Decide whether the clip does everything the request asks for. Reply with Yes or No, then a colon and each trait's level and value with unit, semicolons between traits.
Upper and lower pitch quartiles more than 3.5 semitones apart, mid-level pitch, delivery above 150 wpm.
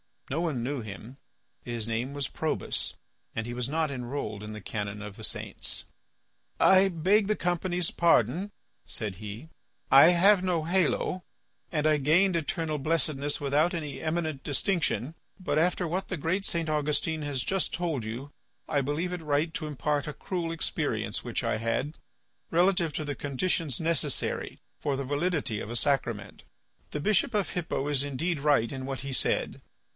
Yes: average, 4.3 semitones; medium, 150 Hz; average, 170 wpm